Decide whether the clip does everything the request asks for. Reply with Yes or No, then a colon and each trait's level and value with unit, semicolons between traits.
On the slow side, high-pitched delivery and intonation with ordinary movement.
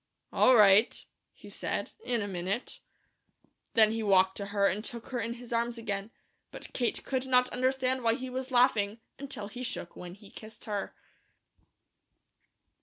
No: average, 165 wpm; high, 230 Hz; average, 3.7 semitones